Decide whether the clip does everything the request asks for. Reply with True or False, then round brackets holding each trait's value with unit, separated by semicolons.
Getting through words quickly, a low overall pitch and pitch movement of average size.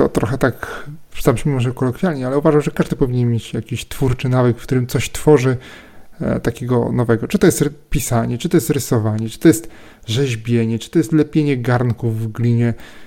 True (190 wpm; 130 Hz; 4.1 semitones)